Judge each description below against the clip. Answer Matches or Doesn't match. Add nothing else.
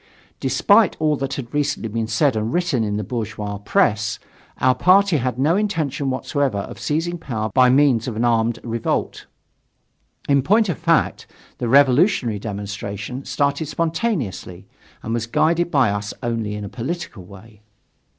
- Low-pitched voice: Matches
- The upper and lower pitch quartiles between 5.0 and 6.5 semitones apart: Matches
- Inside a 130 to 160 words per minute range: Matches